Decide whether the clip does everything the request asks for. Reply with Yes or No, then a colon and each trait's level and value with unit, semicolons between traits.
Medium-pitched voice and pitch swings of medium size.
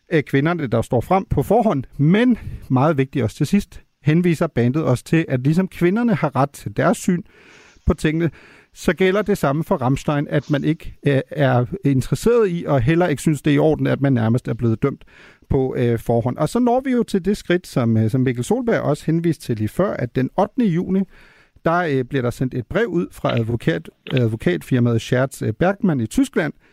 No: medium, 150 Hz; wide, 5.9 semitones